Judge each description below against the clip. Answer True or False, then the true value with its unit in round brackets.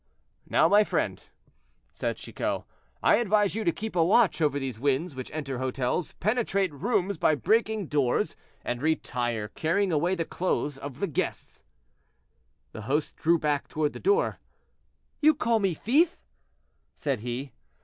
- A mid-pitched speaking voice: True (160 Hz)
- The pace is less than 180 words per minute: True (150 wpm)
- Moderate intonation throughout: False (7.0 semitones)